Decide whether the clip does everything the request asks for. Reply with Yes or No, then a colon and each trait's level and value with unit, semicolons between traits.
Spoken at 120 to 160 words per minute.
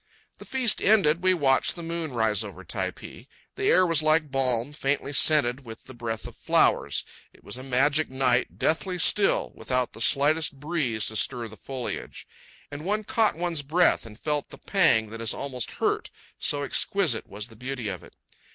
No: average, 185 wpm